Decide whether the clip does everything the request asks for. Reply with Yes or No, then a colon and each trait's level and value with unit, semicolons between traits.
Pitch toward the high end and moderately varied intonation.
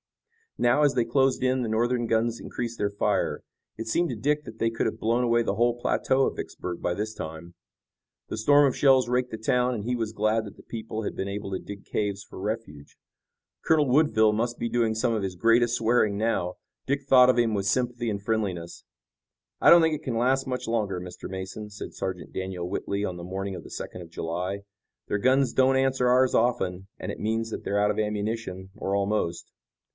No: low, 110 Hz; average, 3.7 semitones